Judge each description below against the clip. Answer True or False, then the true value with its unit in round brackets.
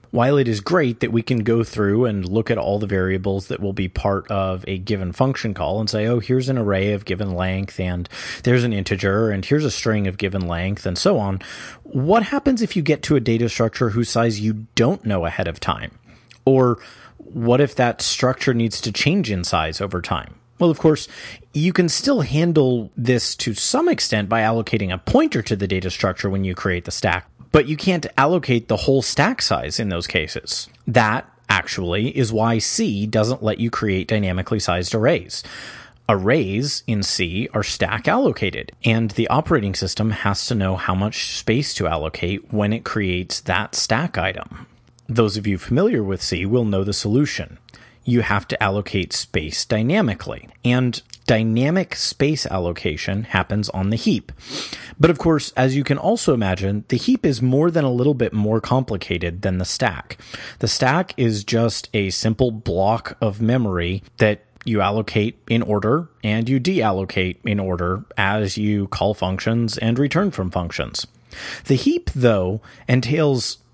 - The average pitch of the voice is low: True (110 Hz)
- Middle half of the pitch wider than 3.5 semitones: True (4.4 semitones)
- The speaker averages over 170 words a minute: True (180 wpm)